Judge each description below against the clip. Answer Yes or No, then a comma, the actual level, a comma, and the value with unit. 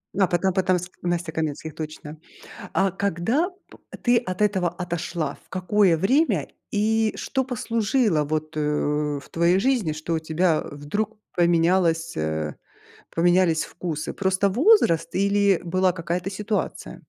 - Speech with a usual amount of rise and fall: Yes, average, 4.0 semitones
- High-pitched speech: No, medium, 180 Hz